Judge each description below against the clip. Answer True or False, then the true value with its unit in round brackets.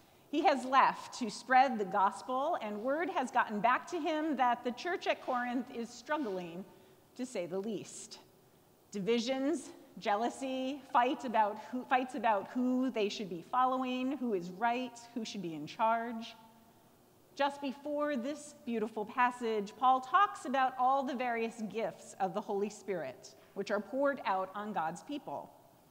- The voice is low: False (245 Hz)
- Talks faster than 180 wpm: False (160 wpm)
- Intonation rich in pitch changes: False (4.2 semitones)